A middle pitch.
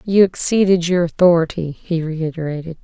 Yes: medium, 170 Hz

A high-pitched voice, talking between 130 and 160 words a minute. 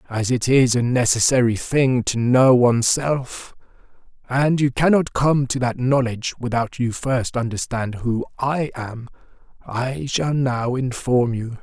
No: low, 125 Hz; average, 150 wpm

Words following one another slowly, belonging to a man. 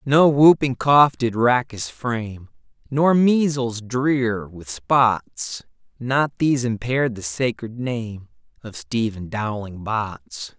Yes: slow, 125 wpm; male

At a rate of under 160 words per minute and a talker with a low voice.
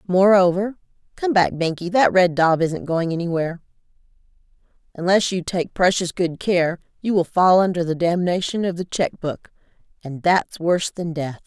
No: average, 150 wpm; medium, 175 Hz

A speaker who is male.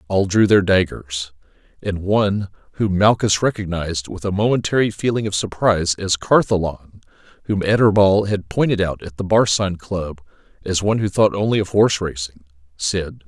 Yes: male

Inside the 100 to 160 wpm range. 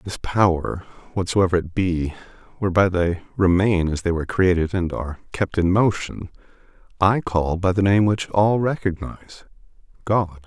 Yes: average, 145 wpm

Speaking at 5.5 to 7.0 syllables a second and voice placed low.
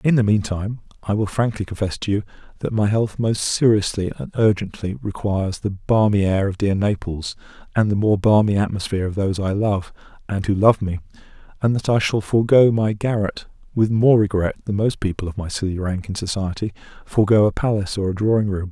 Yes: 5.7 syllables/s; low, 100 Hz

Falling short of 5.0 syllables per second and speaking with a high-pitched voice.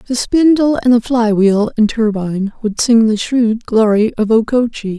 Yes: 4.5 syllables/s; high, 225 Hz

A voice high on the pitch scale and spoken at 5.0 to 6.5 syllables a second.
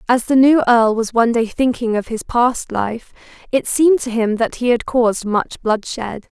No: high, 235 Hz; 4.7 syllables/s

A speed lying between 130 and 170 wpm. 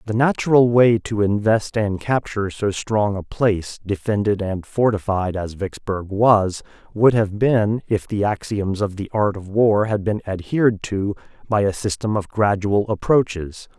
Yes: average, 165 wpm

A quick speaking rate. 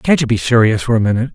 Yes: fast, 310 wpm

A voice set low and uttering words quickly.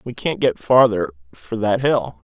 No: low, 110 Hz; average, 180 wpm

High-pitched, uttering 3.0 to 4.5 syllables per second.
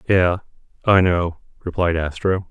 No: very low, 90 Hz; 4.1 syllables/s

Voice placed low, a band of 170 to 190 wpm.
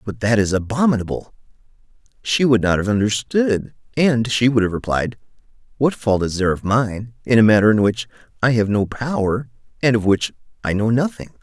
Yes: low, 115 Hz; average, 185 wpm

